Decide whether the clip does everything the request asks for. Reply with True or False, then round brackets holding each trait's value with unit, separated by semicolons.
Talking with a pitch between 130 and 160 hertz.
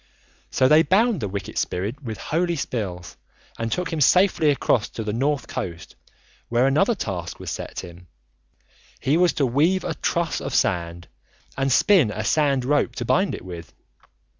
True (135 Hz)